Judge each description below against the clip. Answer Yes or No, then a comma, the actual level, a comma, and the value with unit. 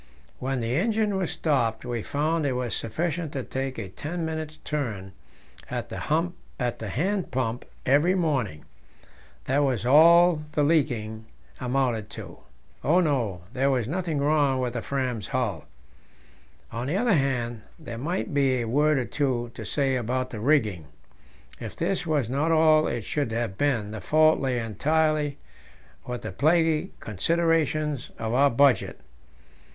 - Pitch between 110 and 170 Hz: Yes, low, 135 Hz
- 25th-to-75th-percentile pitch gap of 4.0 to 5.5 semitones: Yes, average, 4.7 semitones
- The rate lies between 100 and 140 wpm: No, average, 150 wpm